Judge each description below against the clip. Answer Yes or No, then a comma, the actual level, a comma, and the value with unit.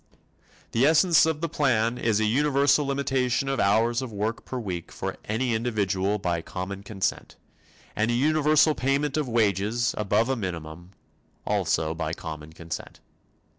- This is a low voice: Yes, low, 115 Hz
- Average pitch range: No, wide, 5.8 semitones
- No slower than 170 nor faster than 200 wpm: No, average, 150 wpm